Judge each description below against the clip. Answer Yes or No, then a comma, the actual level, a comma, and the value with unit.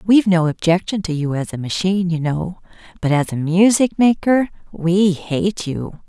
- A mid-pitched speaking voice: Yes, medium, 180 Hz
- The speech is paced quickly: No, average, 180 wpm